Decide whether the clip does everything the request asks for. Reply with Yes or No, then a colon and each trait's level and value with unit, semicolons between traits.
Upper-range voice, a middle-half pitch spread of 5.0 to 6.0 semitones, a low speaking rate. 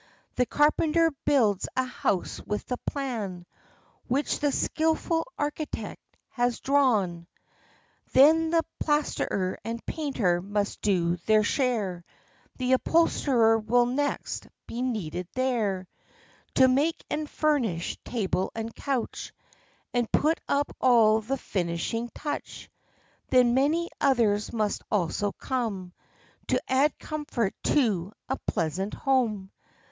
Yes: high, 245 Hz; wide, 5.6 semitones; slow, 115 wpm